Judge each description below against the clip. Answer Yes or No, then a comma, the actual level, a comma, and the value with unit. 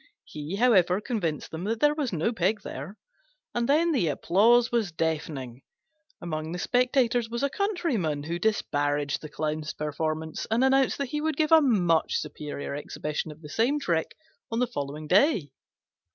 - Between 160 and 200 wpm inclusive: Yes, average, 165 wpm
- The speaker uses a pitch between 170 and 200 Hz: Yes, medium, 185 Hz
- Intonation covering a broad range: Yes, wide, 8.1 semitones